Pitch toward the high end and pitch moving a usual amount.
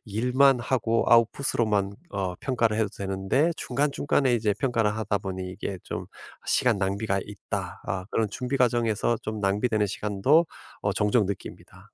No: low, 110 Hz; average, 3.7 semitones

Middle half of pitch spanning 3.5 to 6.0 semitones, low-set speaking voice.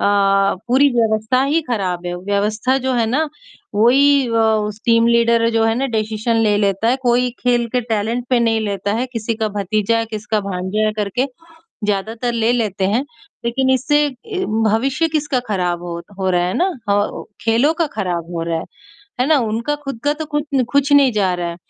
No: average, 3.8 semitones; high, 225 Hz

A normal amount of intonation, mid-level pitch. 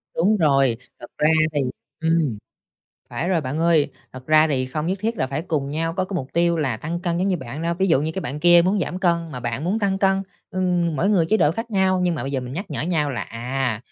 Yes: average, 4.9 semitones; medium, 165 Hz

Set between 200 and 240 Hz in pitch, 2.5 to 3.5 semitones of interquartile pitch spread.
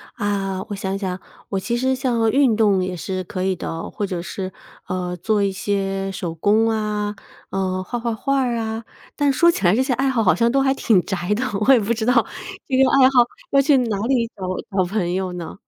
No: high, 210 Hz; average, 4.5 semitones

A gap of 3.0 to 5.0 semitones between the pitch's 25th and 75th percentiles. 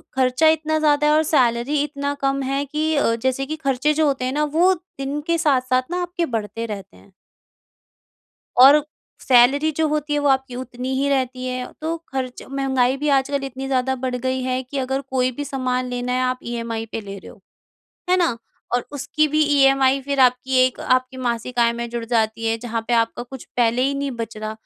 No: narrow, 2.5 semitones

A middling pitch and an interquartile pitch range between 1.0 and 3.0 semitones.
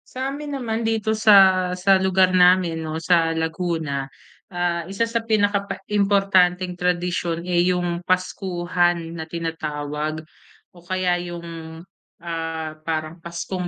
Yes: medium, 175 Hz; narrow, 2.4 semitones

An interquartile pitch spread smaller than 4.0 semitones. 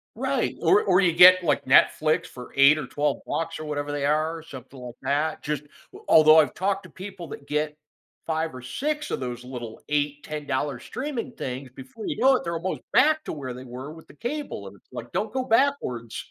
No: average, 5.2 semitones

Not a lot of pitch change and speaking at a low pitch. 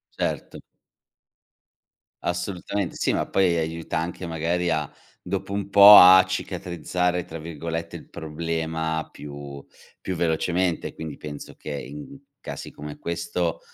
Yes: narrow, 2.1 semitones; very low, 85 Hz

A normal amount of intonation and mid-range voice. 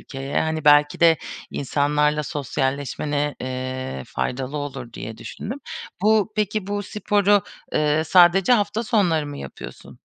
No: wide, 6.2 semitones; medium, 150 Hz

